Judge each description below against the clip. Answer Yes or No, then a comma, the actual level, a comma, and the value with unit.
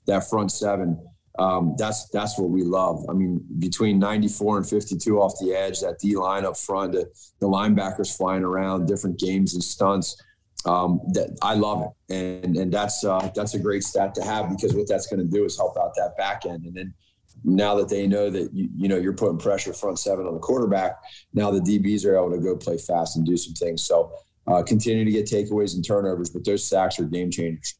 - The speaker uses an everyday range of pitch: No, narrow, 2.2 semitones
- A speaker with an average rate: No, fast, 230 wpm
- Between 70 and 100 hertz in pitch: Yes, very low, 95 Hz